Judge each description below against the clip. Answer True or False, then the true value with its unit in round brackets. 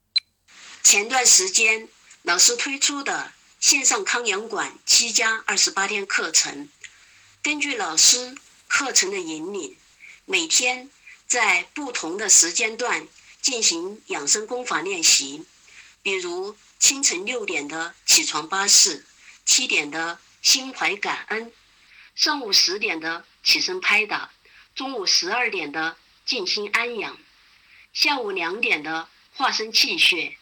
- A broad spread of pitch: True (8.3 semitones)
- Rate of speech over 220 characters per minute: False (185 characters per minute)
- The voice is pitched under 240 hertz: False (265 Hz)